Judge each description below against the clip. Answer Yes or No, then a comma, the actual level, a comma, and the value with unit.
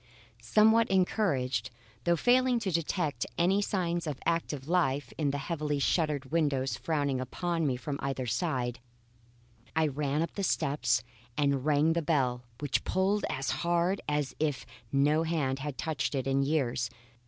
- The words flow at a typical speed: Yes, average, 155 wpm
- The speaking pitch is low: No, medium, 150 Hz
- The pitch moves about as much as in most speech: Yes, average, 4.0 semitones